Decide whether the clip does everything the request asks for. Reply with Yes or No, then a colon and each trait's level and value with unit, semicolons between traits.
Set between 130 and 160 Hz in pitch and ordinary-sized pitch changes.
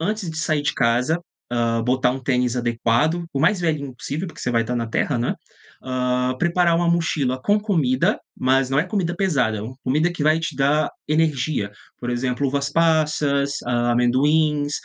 Yes: medium, 140 Hz; average, 4.4 semitones